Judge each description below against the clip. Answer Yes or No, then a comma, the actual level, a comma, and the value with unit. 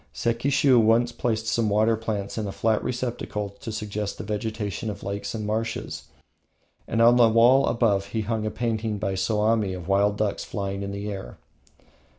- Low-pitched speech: Yes, low, 110 Hz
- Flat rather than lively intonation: Yes, narrow, 2.1 semitones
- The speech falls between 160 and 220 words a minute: Yes, average, 175 wpm